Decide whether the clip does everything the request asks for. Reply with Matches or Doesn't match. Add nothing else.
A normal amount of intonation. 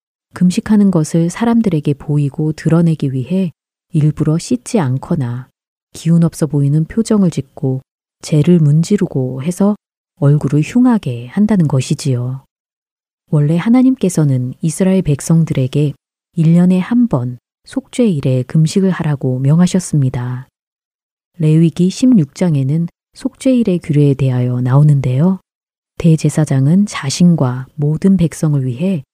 Matches